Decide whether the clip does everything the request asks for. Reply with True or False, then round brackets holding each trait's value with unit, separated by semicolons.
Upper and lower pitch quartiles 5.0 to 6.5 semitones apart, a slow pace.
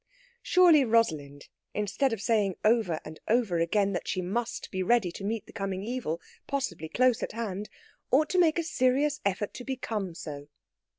False (5.5 semitones; 175 wpm)